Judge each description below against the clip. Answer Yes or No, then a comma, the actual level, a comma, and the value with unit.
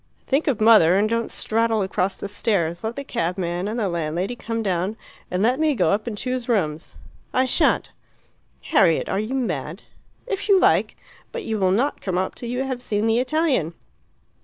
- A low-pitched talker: No, high, 215 Hz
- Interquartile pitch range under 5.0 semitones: No, average, 5.3 semitones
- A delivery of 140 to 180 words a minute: No, average, 190 wpm